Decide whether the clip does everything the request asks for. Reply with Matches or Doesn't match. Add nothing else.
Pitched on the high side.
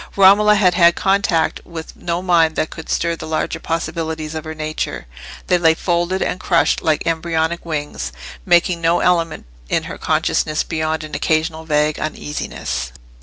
Doesn't match